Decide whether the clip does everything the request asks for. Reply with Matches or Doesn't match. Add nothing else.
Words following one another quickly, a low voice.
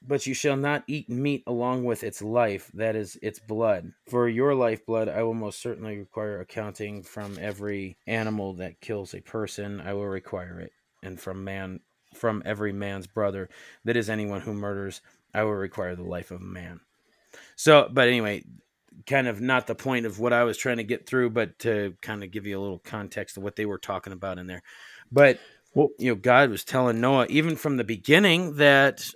Matches